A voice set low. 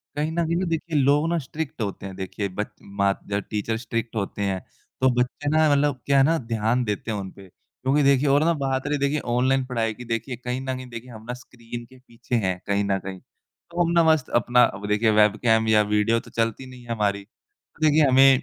Yes: low, 125 Hz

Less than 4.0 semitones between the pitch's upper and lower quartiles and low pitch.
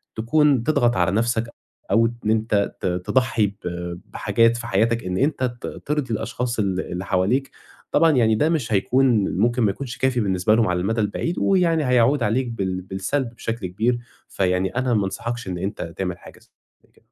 No: average, 4.5 semitones; low, 115 Hz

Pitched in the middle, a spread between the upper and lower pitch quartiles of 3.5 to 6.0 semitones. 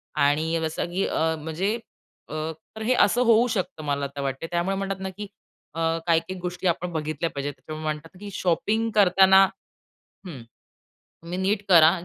Yes: medium, 175 Hz; average, 3.8 semitones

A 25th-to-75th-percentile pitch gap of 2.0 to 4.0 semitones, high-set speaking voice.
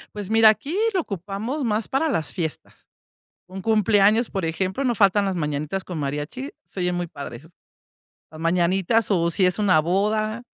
No: average, 4.4 semitones; high, 195 Hz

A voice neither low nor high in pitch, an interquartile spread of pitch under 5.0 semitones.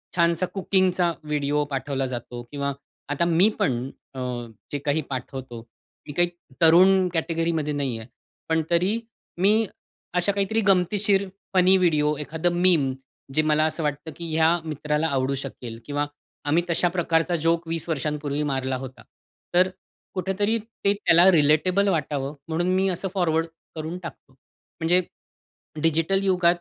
Yes: medium, 165 Hz; average, 3.8 semitones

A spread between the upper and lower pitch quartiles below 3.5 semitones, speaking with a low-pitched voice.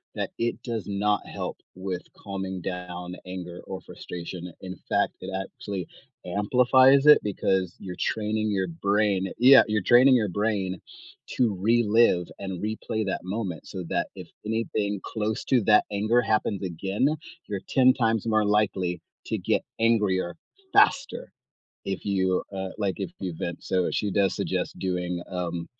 Yes: average, 3.0 semitones; low, 100 Hz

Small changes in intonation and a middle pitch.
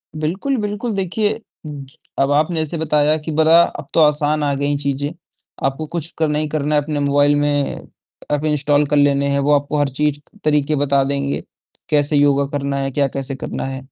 Yes: narrow, 1.7 semitones; medium, 145 Hz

